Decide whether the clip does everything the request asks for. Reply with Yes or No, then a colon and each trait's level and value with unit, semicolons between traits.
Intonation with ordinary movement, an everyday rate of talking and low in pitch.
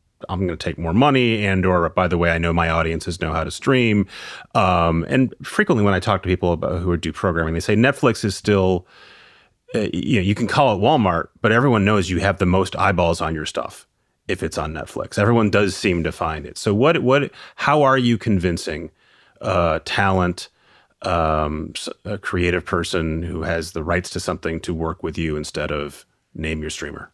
No: average, 3.7 semitones; fast, 210 wpm; very low, 90 Hz